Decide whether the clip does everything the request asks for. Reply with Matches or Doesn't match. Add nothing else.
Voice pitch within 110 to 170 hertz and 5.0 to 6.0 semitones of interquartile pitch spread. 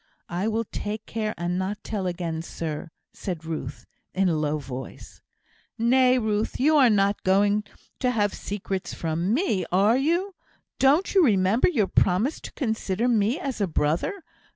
Doesn't match